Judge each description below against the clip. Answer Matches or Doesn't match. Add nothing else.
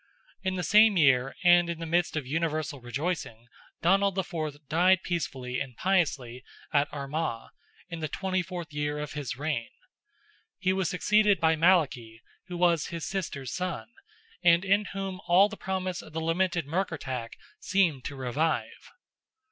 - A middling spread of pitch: Matches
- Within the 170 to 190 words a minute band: Doesn't match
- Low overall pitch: Doesn't match